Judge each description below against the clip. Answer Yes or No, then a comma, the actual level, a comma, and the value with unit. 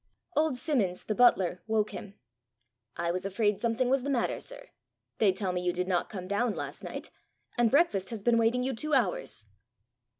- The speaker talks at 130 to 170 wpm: No, average, 190 wpm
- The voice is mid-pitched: No, high, 220 Hz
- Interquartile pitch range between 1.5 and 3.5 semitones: No, average, 4.9 semitones